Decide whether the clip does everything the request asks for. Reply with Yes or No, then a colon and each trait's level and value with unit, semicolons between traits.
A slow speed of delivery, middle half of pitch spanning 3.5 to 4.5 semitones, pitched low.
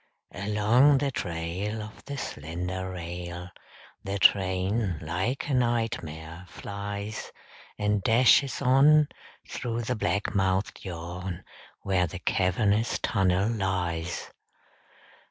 Yes: slow, 100 wpm; average, 4.1 semitones; low, 100 Hz